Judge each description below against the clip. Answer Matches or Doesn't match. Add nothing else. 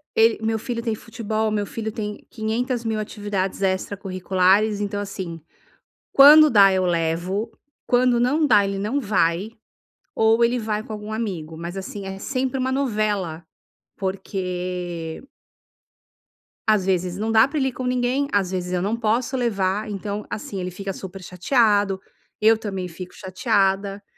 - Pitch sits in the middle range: Doesn't match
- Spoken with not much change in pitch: Doesn't match